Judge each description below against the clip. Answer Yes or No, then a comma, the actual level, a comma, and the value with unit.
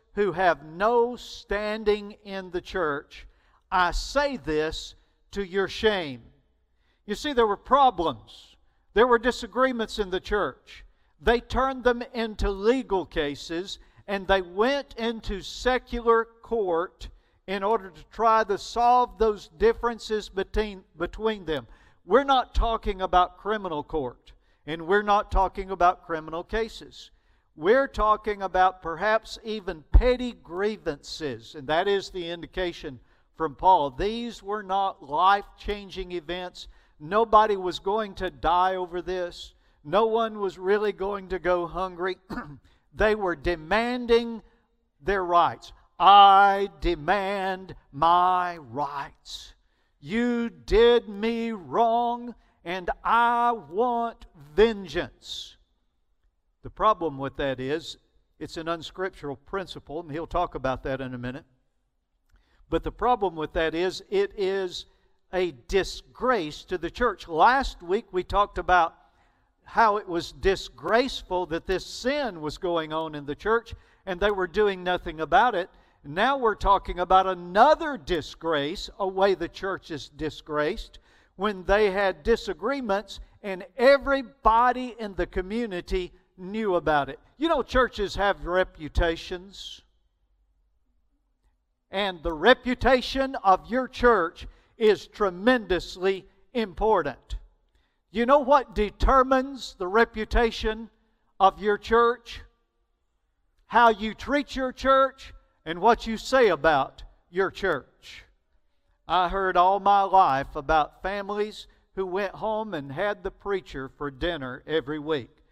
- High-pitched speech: Yes, high, 195 Hz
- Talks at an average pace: No, slow, 125 wpm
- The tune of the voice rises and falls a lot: No, average, 4.8 semitones